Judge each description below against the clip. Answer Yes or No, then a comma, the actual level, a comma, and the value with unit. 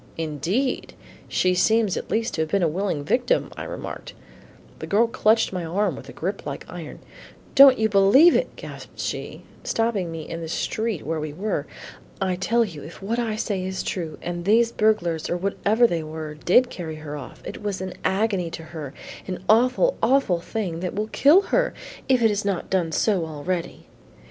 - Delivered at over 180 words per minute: Yes, average, 195 wpm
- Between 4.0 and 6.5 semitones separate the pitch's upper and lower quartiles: Yes, average, 5.2 semitones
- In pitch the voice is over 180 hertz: Yes, high, 190 Hz